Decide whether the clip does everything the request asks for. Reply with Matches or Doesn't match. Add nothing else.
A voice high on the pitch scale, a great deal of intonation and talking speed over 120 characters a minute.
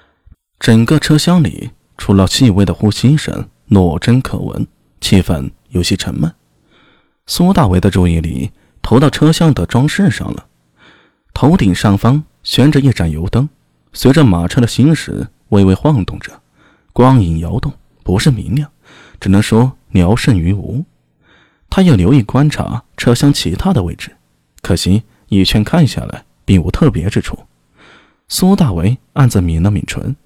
Doesn't match